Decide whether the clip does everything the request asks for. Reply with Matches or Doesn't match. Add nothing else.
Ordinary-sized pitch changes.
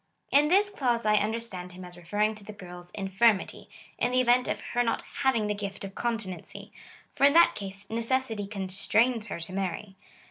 Matches